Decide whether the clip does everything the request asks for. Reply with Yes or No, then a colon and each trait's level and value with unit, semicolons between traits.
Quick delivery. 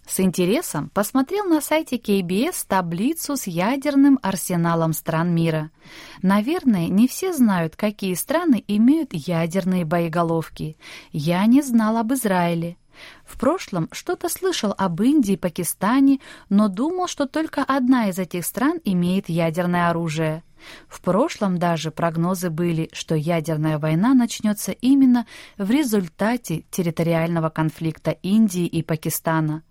No: average, 125 wpm